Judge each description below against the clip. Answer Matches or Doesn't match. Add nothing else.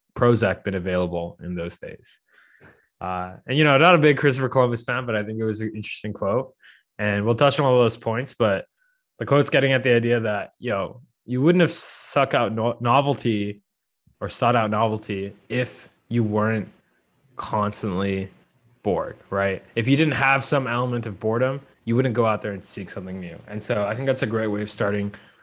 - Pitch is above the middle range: Doesn't match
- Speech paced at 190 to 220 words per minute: Matches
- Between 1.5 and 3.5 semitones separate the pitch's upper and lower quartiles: Doesn't match